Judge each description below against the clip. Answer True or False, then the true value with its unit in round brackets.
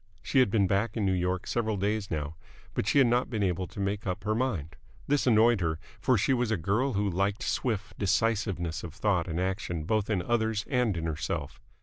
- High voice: False (100 Hz)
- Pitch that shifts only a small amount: False (3.8 semitones)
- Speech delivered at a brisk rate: True (220 wpm)